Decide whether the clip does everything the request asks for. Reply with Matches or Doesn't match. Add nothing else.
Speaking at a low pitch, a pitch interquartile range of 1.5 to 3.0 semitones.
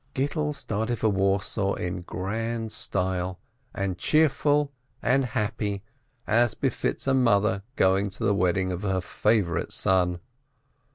Doesn't match